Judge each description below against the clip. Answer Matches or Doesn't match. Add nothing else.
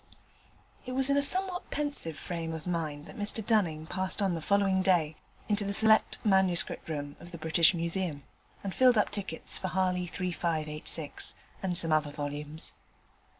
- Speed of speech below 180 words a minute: Matches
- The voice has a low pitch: Doesn't match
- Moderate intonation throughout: Matches